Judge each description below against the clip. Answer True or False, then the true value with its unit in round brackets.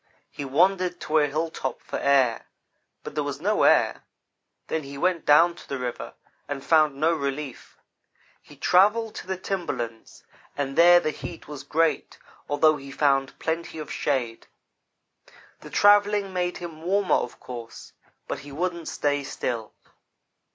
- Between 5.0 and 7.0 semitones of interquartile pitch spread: False (4.2 semitones)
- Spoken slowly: False (155 wpm)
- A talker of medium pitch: True (155 Hz)